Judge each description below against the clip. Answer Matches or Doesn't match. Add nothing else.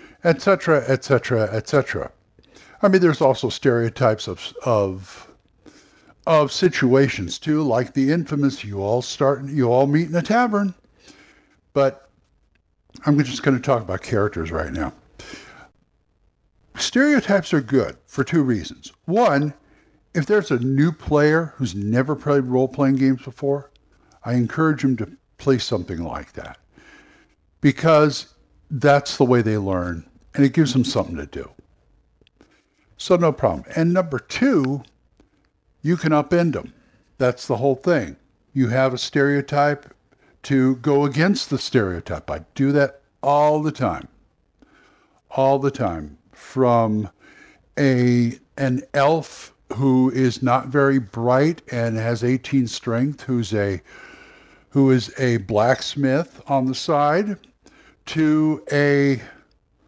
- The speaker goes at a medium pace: Doesn't match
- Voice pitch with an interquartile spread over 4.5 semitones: Doesn't match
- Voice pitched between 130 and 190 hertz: Matches